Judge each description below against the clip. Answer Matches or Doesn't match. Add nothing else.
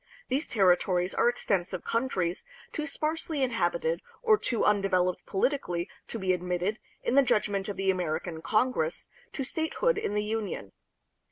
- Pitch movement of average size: Doesn't match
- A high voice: Matches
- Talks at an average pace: Matches